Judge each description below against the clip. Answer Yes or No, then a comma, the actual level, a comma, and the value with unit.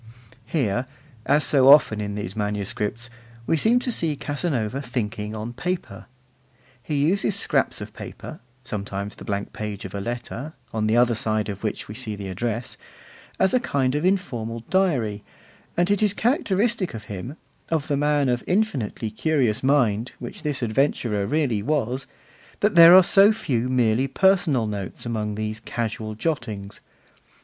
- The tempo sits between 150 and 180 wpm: Yes, average, 160 wpm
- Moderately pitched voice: No, low, 120 Hz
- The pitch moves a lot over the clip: Yes, wide, 6.3 semitones